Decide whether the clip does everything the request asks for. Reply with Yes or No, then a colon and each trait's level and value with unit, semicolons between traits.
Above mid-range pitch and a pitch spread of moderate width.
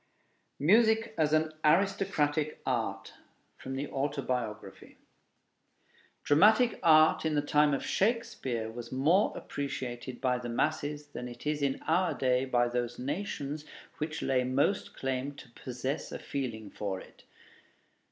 No: medium, 140 Hz; average, 3.9 semitones